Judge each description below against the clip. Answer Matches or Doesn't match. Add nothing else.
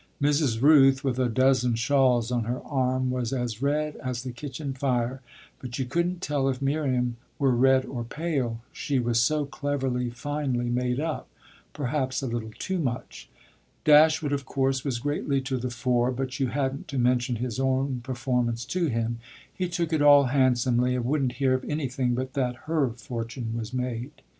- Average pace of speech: Matches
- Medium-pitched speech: Doesn't match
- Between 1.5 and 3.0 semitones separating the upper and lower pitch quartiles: Matches